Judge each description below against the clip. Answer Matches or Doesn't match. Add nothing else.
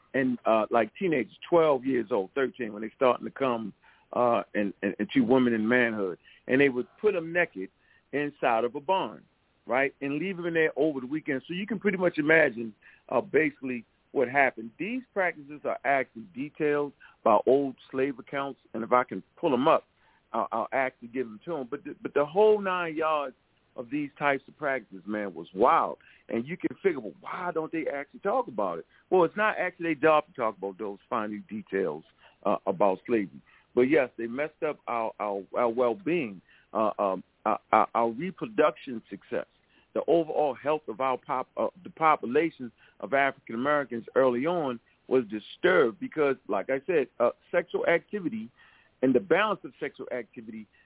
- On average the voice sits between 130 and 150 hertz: Matches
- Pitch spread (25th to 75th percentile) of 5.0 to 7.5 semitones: Matches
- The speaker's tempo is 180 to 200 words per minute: Matches